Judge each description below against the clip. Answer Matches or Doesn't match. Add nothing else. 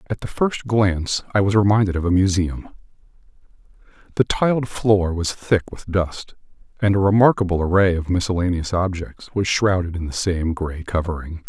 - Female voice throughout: Doesn't match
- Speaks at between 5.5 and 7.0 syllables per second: Doesn't match